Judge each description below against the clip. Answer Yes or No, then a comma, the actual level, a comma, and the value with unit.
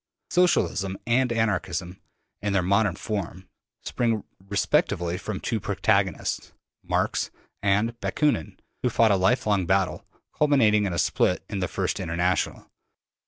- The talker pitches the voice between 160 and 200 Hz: No, low, 100 Hz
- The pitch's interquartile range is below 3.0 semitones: No, average, 3.4 semitones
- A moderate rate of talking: No, slow, 125 wpm